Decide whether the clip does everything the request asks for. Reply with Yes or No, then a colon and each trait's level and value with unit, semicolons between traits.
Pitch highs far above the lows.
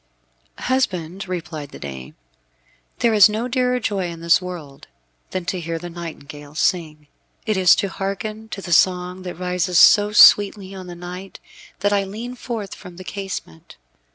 No: average, 3.1 semitones